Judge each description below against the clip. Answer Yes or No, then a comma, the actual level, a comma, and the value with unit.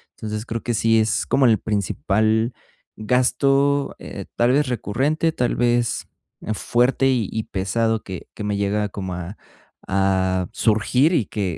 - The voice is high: No, low, 110 Hz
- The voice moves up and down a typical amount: Yes, average, 3.6 semitones